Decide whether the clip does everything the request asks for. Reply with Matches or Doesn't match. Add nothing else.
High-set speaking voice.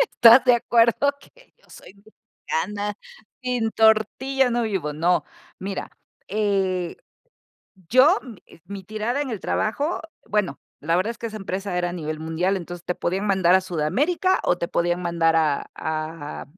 Matches